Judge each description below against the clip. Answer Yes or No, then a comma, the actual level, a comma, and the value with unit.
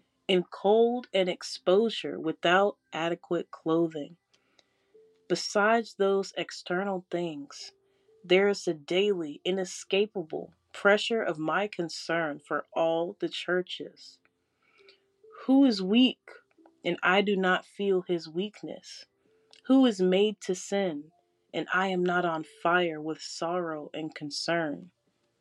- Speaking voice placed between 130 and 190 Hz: Yes, medium, 185 Hz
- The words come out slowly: Yes, slow, 115 wpm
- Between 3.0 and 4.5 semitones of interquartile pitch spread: Yes, average, 3.8 semitones